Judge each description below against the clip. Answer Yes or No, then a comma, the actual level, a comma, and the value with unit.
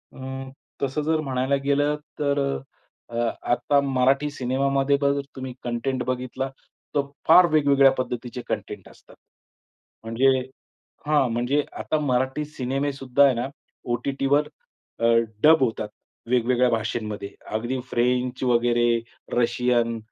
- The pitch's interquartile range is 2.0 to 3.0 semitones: Yes, narrow, 2.5 semitones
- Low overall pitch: Yes, low, 130 Hz